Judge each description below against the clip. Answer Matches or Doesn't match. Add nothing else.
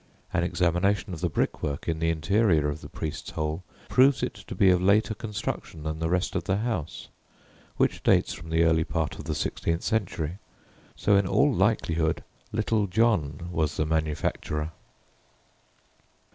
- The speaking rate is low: Doesn't match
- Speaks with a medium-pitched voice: Doesn't match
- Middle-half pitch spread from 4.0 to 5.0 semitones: Matches